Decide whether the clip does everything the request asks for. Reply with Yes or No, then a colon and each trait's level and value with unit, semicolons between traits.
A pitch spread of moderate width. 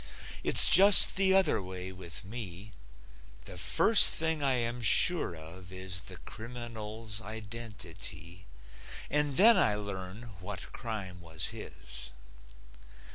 Yes: average, 4.6 semitones